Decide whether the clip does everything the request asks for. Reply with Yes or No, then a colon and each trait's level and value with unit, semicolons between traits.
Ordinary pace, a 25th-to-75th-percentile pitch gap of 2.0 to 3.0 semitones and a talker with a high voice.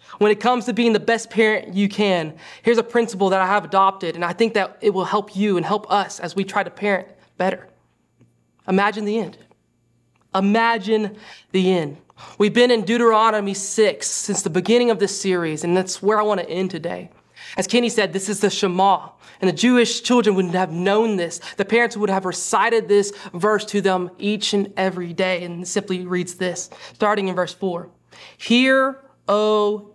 Yes: average, 195 wpm; average, 2.7 semitones; high, 200 Hz